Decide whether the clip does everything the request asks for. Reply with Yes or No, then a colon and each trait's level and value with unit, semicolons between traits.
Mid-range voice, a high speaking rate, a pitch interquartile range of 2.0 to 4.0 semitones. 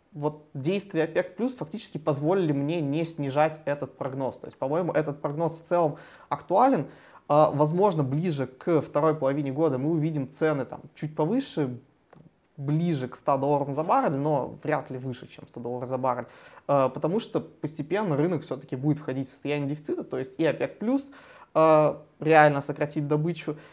Yes: medium, 150 Hz; fast, 160 wpm; narrow, 2.4 semitones